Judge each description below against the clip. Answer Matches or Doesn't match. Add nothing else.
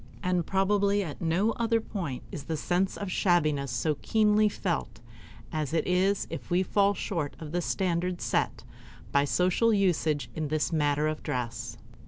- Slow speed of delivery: Doesn't match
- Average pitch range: Matches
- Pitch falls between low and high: Matches